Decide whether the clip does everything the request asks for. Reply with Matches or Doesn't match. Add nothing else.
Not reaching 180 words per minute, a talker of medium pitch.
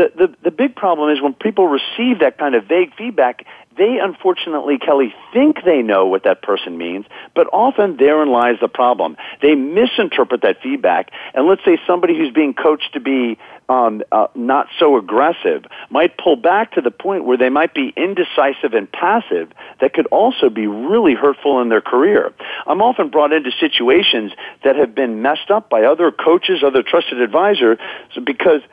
Doesn't match